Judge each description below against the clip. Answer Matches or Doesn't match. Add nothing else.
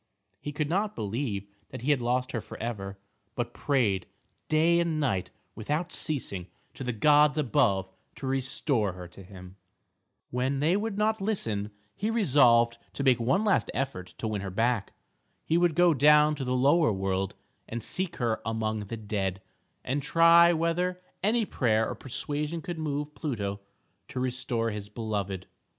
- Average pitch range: Doesn't match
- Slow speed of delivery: Doesn't match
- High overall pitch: Doesn't match